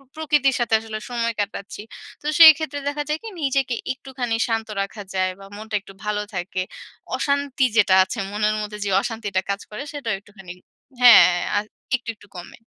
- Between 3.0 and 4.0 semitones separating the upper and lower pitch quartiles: No, average, 4.7 semitones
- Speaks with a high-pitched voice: Yes, high, 225 Hz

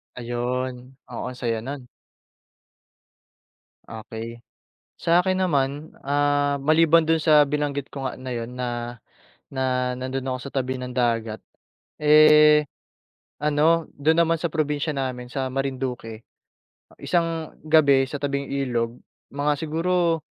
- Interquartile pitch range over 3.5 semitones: No, average, 3.2 semitones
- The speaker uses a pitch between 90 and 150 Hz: Yes, medium, 140 Hz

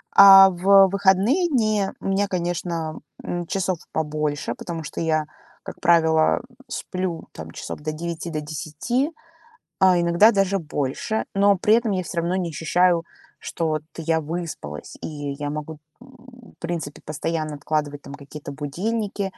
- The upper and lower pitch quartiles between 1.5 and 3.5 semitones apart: No, average, 4.1 semitones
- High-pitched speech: No, medium, 170 Hz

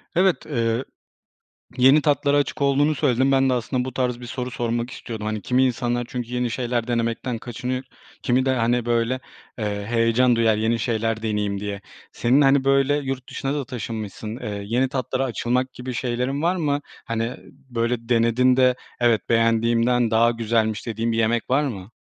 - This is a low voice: Yes, low, 120 Hz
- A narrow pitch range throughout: Yes, narrow, 2.2 semitones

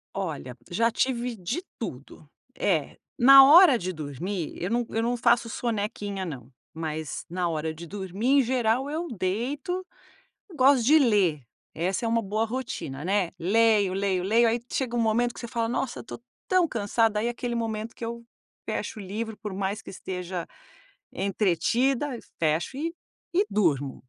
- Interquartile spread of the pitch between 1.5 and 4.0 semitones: No, average, 4.8 semitones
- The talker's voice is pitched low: No, high, 220 Hz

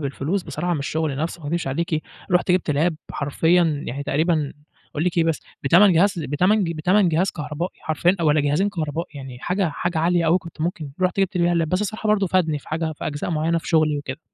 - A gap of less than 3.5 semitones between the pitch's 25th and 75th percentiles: Yes, average, 3.0 semitones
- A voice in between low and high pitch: Yes, medium, 165 Hz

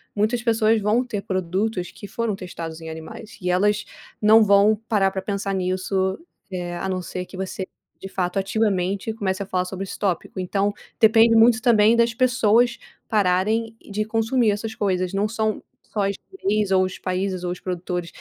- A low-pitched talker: No, high, 200 Hz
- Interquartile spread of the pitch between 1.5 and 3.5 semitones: Yes, average, 3.0 semitones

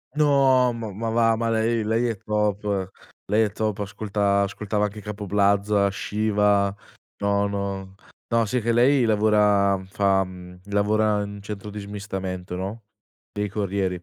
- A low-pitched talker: Yes, low, 105 Hz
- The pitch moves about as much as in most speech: No, narrow, 1.7 semitones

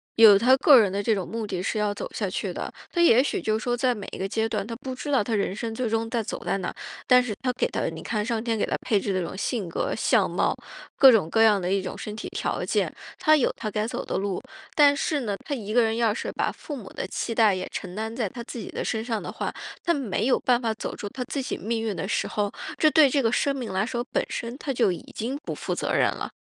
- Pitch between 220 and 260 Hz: Yes, high, 225 Hz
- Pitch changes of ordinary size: Yes, average, 3.5 semitones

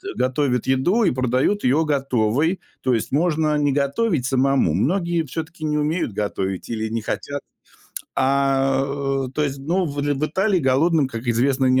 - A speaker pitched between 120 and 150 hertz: Yes, medium, 140 Hz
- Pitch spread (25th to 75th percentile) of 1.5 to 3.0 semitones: No, average, 3.5 semitones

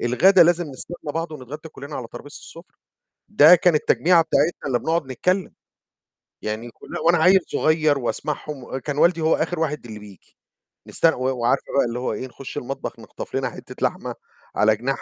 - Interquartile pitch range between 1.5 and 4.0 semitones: No, average, 4.6 semitones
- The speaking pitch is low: No, medium, 150 Hz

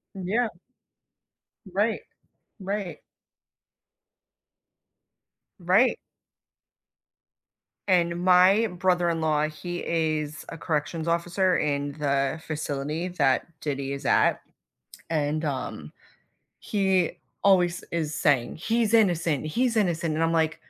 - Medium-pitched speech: Yes, medium, 170 Hz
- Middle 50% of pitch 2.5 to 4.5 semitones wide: Yes, average, 3.5 semitones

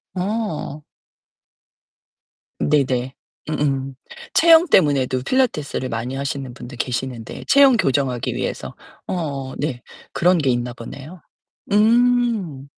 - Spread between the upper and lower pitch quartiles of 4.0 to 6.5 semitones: No, wide, 7.0 semitones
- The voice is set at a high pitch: No, medium, 140 Hz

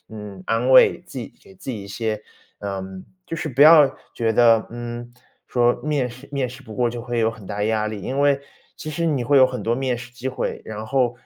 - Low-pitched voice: Yes, low, 120 Hz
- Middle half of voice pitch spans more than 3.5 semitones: No, average, 3.1 semitones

